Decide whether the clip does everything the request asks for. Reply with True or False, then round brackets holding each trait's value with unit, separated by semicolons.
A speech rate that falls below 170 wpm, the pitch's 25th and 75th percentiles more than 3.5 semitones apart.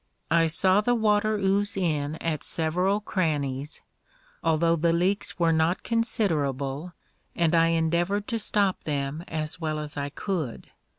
True (140 wpm; 4.1 semitones)